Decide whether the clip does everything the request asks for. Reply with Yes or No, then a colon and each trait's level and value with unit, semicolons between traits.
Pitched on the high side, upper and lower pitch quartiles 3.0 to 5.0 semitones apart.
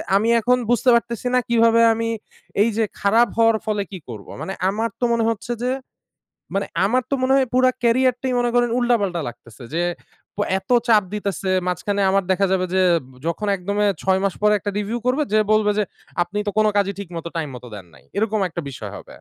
Yes: high, 210 Hz; average, 3.5 semitones